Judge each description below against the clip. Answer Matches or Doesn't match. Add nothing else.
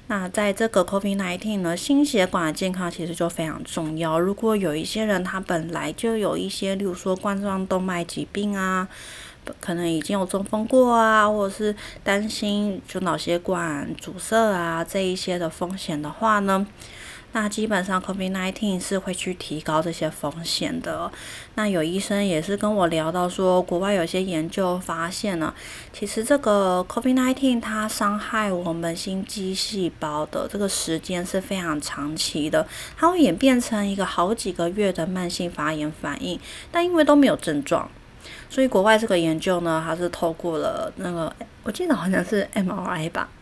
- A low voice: Doesn't match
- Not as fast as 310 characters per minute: Matches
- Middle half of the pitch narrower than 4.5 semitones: Matches